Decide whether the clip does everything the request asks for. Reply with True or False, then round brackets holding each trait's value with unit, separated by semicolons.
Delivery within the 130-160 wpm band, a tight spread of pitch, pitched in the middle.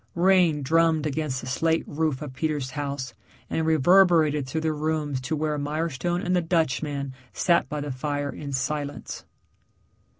True (155 wpm; 2.3 semitones; 150 Hz)